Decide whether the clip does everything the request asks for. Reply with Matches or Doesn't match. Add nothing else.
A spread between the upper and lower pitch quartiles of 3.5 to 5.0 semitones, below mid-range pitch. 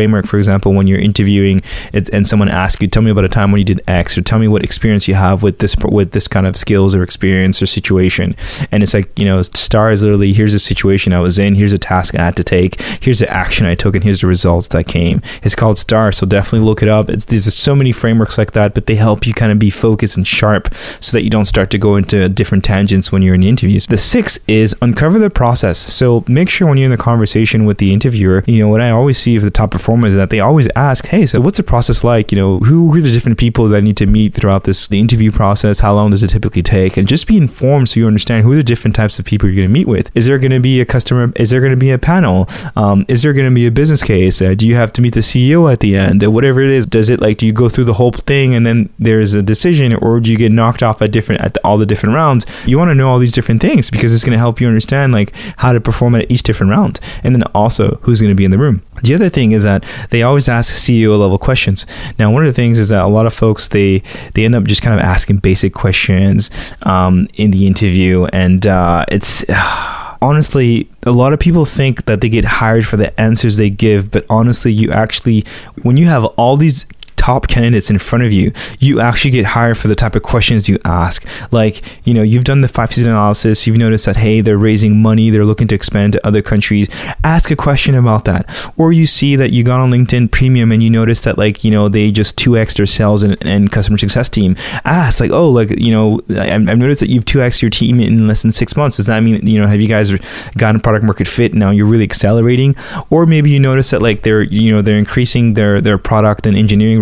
Doesn't match